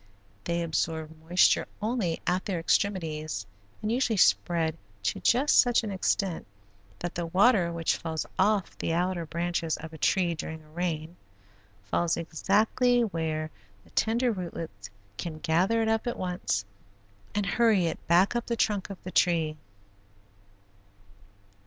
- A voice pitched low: No, medium, 175 Hz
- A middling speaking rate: Yes, average, 145 wpm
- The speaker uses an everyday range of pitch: Yes, average, 4.2 semitones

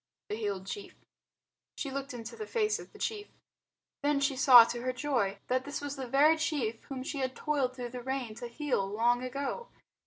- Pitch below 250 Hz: No, very high, 260 Hz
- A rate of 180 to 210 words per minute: Yes, fast, 205 wpm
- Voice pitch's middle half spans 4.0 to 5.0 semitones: No, average, 3.2 semitones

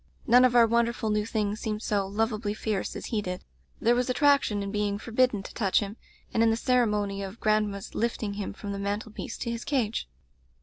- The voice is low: No, high, 215 Hz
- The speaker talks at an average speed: No, fast, 215 wpm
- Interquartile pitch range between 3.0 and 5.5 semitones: No, narrow, 2.4 semitones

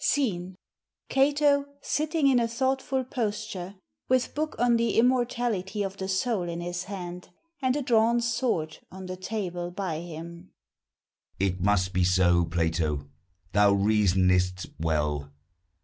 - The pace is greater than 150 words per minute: No, slow, 135 wpm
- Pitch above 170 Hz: Yes, medium, 185 Hz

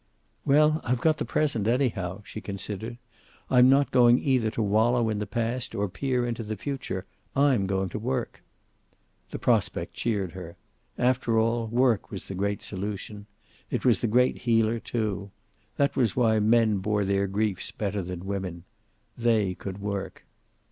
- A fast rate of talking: No, average, 160 wpm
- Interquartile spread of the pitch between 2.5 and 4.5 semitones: Yes, average, 3.5 semitones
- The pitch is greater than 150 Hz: No, low, 110 Hz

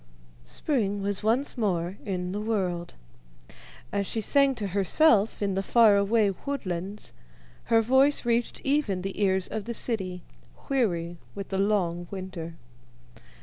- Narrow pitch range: No, average, 3.7 semitones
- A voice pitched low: No, high, 200 Hz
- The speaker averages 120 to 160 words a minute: Yes, slow, 135 wpm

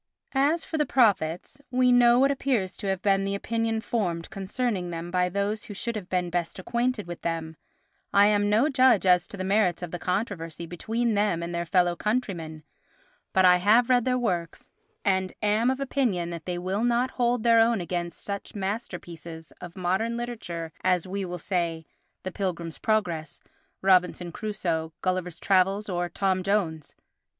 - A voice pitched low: No, high, 190 Hz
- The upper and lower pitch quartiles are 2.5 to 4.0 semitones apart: No, average, 4.5 semitones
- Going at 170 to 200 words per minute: Yes, average, 175 wpm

